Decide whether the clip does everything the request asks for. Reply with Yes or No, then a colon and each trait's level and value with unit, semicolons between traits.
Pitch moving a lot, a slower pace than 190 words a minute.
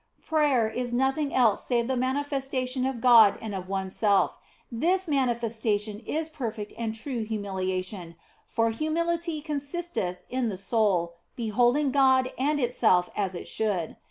No: average, 4.8 semitones; average, 145 wpm